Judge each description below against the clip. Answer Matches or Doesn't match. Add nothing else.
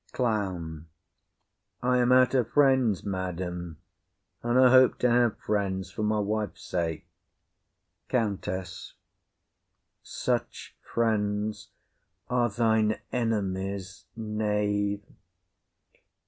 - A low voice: Matches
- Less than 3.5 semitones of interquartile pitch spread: Doesn't match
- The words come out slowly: Matches